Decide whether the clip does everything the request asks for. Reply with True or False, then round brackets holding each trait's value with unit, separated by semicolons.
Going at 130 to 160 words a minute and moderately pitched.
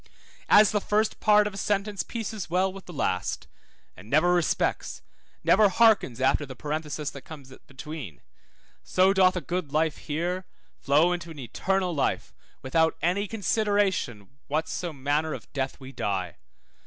True (155 wpm; 165 Hz)